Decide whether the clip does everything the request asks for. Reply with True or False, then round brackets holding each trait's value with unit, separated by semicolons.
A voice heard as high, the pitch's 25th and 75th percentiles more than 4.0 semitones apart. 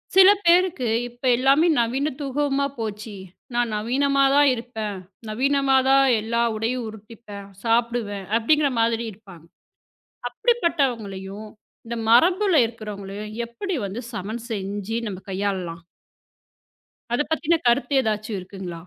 True (235 Hz; 4.7 semitones)